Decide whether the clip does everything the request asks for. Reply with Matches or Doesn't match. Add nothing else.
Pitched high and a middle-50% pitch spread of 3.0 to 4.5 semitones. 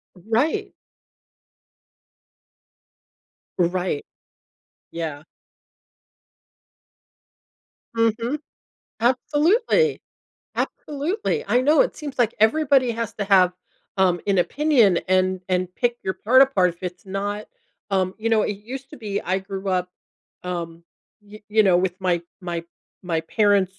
Doesn't match